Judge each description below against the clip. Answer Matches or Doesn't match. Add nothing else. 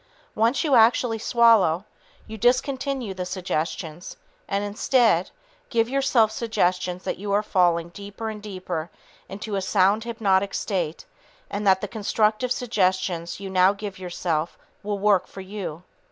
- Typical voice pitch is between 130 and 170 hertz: Doesn't match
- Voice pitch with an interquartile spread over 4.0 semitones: Doesn't match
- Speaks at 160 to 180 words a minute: Doesn't match